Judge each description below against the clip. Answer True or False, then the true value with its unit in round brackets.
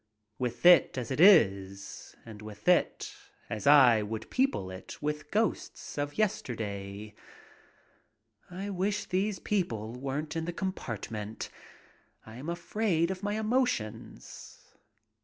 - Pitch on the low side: False (145 Hz)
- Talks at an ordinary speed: False (120 wpm)